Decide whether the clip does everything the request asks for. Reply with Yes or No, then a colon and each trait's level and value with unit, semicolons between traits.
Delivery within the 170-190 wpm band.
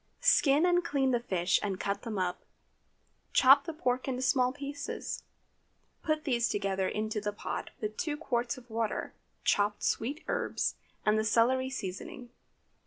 No: average, 155 wpm